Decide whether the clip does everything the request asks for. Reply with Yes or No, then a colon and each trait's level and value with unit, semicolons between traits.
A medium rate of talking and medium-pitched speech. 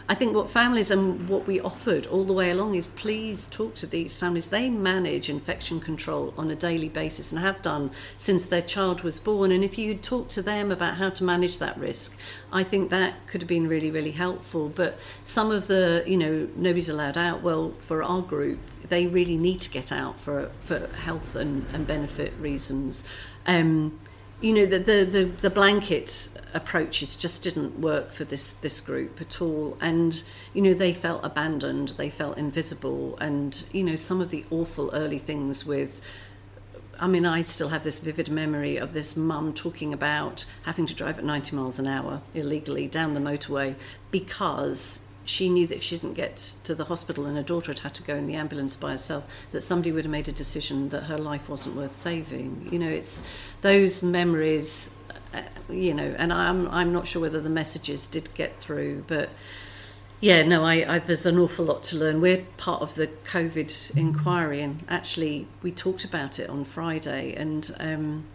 Yes: average, 195 wpm; medium, 160 Hz